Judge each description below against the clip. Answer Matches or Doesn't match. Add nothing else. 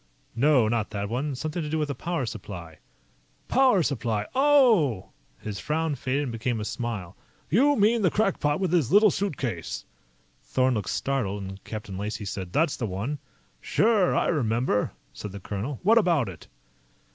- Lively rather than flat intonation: Matches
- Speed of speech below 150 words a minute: Doesn't match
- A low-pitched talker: Matches